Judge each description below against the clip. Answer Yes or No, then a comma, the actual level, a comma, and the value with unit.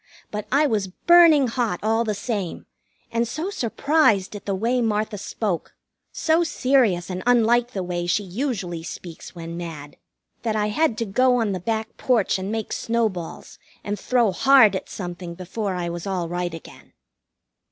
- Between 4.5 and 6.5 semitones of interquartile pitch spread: Yes, average, 4.9 semitones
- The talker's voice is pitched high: Yes, high, 210 Hz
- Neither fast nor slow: Yes, average, 170 wpm